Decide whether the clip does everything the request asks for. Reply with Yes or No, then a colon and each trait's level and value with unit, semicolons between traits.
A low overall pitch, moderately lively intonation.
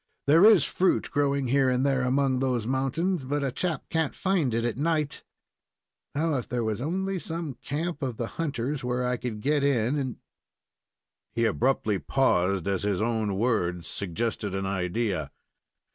Yes: low, 130 Hz; average, 4.7 semitones